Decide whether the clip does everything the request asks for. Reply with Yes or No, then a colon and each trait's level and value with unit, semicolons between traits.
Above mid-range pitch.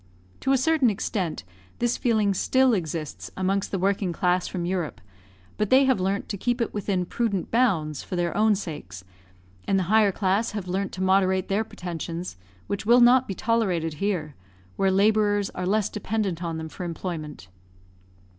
Yes: high, 195 Hz